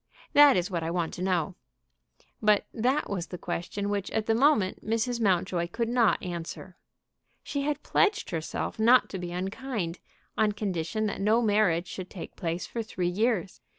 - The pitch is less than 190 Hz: No, high, 200 Hz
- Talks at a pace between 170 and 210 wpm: Yes, average, 175 wpm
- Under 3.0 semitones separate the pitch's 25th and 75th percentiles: No, average, 4.4 semitones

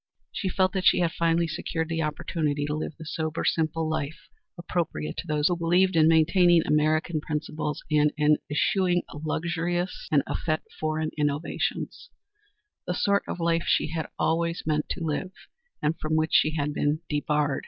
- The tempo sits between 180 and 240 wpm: No, average, 165 wpm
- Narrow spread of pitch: Yes, narrow, 2.0 semitones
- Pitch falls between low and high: Yes, medium, 160 Hz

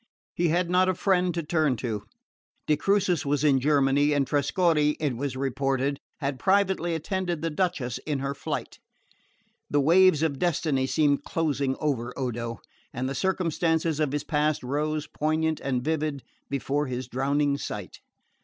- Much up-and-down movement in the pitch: No, average, 3.2 semitones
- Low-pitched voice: No, medium, 150 Hz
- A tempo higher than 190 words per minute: No, average, 155 wpm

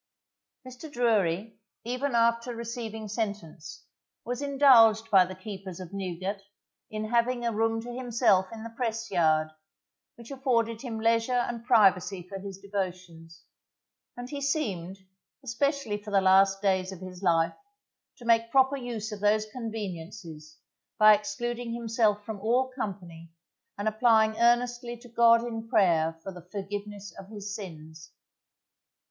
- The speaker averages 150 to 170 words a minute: No, average, 140 wpm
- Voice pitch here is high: Yes, high, 215 Hz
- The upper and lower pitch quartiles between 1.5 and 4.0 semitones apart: Yes, average, 3.7 semitones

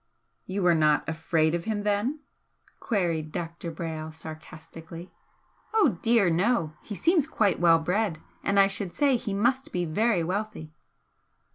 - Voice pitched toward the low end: No, medium, 180 Hz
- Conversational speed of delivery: Yes, average, 145 wpm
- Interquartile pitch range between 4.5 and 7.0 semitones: Yes, average, 4.9 semitones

